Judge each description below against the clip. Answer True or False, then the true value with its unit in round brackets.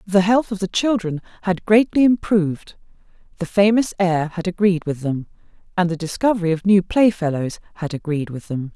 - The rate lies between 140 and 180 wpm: True (170 wpm)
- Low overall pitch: False (185 Hz)